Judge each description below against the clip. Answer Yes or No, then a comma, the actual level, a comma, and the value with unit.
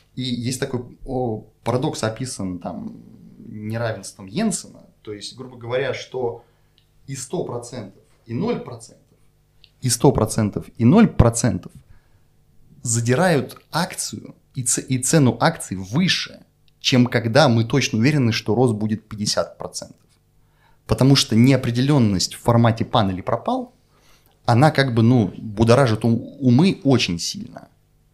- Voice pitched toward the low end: Yes, low, 120 Hz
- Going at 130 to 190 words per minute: No, average, 115 wpm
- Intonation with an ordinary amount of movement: Yes, average, 3.3 semitones